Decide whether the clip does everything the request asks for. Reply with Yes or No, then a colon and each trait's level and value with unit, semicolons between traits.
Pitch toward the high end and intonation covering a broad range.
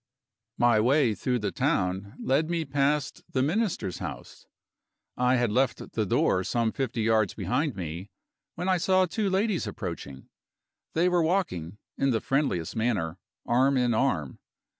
No: low, 125 Hz; wide, 7.0 semitones